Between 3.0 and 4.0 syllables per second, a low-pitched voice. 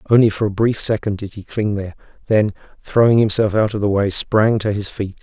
No: 5.8 syllables/s; low, 105 Hz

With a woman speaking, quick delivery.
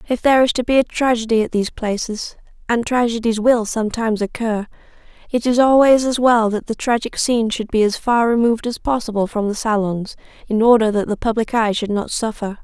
No: female; average, 195 wpm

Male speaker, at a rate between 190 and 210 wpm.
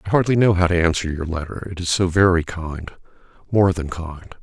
Yes: male; fast, 205 wpm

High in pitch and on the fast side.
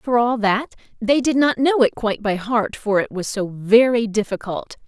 Yes: high, 225 Hz; fast, 210 wpm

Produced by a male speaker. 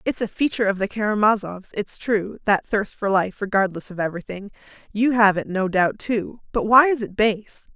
No: female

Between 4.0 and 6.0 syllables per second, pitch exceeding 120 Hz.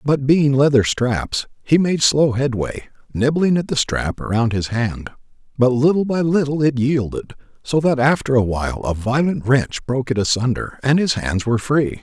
Yes: 4.8 syllables/s; low, 135 Hz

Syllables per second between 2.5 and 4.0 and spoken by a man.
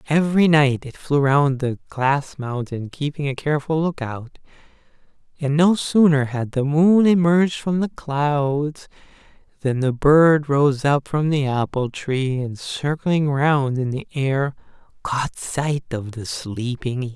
Yes: 3.9 syllables/s; male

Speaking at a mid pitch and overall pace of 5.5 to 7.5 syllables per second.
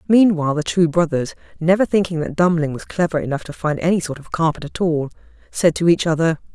Yes: medium, 165 Hz; 6.1 syllables/s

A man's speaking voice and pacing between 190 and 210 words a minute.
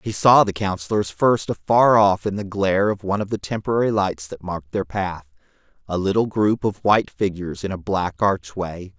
Yes: male; average, 200 wpm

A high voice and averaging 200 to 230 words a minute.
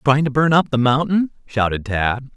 No: low, 135 Hz; fast, 205 wpm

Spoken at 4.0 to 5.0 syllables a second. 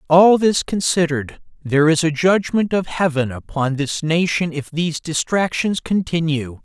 Yes: 4.7 syllables/s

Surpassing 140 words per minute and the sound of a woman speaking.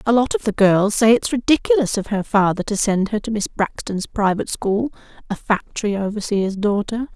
Yes: average, 195 wpm; female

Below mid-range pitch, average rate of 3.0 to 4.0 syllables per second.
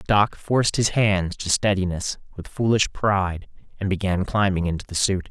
No: low, 100 Hz; 4.9 syllables/s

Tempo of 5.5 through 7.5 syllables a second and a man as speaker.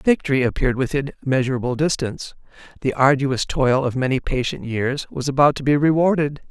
Yes: 5.7 syllables/s; male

